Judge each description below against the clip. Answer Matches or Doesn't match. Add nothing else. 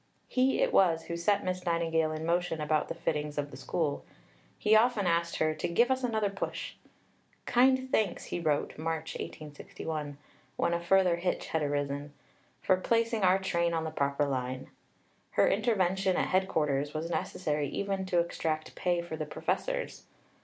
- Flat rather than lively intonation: Doesn't match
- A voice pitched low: Doesn't match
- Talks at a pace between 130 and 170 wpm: Matches